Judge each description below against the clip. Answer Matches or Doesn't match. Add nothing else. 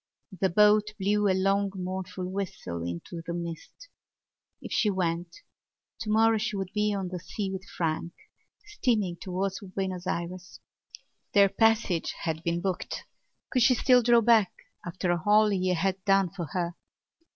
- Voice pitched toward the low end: Doesn't match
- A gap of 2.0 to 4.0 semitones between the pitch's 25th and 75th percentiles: Matches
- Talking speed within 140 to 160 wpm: Matches